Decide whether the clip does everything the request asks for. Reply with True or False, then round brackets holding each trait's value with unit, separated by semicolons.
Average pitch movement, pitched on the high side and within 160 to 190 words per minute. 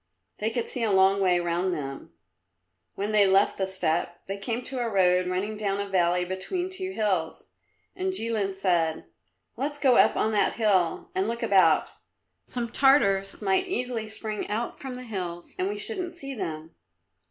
True (5.0 semitones; 205 Hz; 175 wpm)